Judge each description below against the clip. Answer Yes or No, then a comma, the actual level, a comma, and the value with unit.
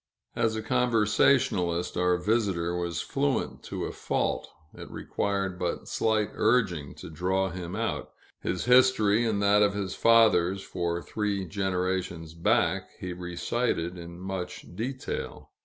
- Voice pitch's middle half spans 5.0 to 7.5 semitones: No, average, 3.7 semitones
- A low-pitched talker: Yes, very low, 95 Hz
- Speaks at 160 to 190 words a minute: No, slow, 135 wpm